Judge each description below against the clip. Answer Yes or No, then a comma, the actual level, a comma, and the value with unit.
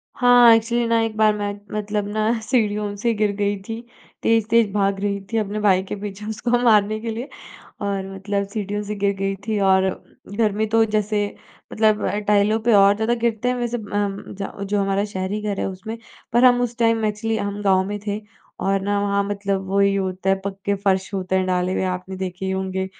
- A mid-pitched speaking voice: No, high, 205 Hz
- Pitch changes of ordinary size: No, narrow, 2.0 semitones